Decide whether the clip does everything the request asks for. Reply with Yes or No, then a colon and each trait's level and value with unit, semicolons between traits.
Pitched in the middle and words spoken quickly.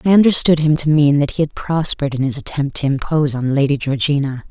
Yes: medium, 145 Hz; fast, 225 wpm